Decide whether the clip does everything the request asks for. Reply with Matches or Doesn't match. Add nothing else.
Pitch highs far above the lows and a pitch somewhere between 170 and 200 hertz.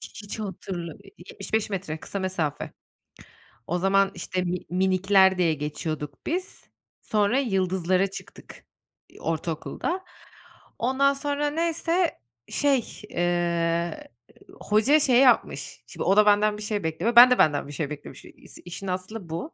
Matches